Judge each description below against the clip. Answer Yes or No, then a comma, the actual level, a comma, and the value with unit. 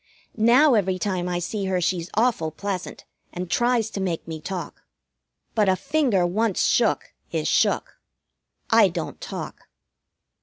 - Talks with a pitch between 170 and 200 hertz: Yes, high, 190 Hz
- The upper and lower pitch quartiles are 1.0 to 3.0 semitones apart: No, average, 3.8 semitones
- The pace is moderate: Yes, average, 145 wpm